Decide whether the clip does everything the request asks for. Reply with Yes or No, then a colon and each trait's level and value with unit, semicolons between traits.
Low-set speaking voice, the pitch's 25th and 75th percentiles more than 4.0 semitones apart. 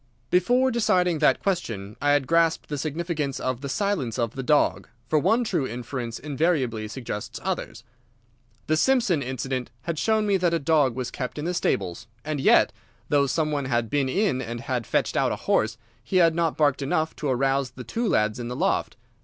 No: medium, 145 Hz; average, 5.1 semitones